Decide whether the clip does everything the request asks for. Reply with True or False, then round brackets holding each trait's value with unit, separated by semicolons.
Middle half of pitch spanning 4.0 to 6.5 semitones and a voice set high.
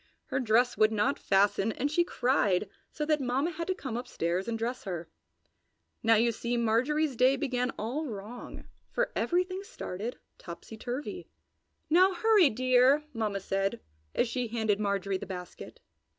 True (5.1 semitones; 240 Hz)